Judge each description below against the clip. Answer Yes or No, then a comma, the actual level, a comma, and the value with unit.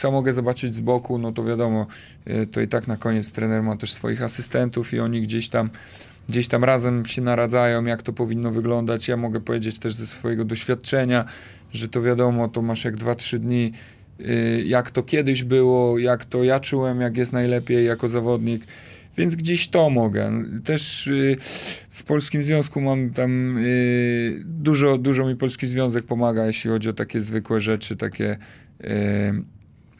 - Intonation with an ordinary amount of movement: No, narrow, 2.0 semitones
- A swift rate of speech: Yes, fast, 165 wpm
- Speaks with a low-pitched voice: Yes, low, 120 Hz